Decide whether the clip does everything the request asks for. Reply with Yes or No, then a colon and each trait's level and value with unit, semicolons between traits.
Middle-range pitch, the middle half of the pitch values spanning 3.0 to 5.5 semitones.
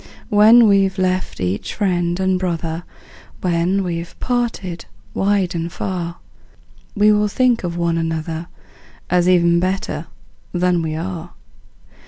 No: medium, 180 Hz; narrow, 2.4 semitones